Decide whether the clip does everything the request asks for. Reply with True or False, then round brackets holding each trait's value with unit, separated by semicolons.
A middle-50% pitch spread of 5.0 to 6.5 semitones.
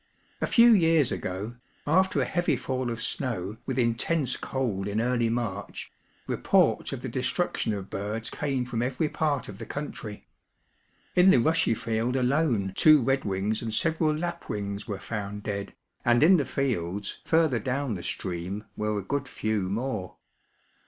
True (5.6 semitones)